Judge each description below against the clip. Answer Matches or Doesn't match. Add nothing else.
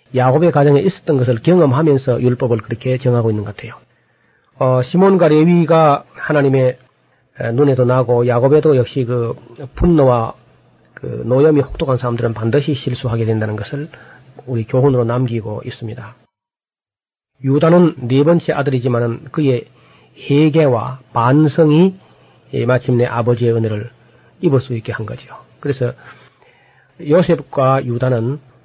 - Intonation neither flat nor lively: Matches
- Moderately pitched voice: Doesn't match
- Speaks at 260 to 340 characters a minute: Matches